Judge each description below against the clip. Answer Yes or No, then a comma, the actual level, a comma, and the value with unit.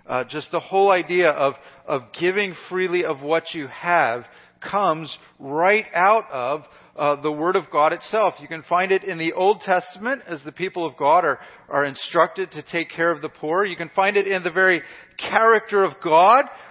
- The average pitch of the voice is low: No, medium, 170 Hz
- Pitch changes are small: No, average, 3.7 semitones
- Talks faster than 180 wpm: Yes, average, 200 wpm